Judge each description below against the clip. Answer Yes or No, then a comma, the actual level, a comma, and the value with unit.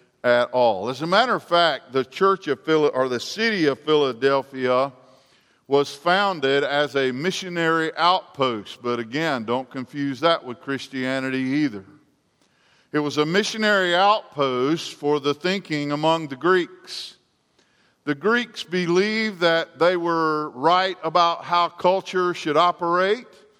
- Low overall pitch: No, medium, 155 Hz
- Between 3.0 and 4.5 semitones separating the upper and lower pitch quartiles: No, average, 5.0 semitones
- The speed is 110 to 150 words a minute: Yes, slow, 135 wpm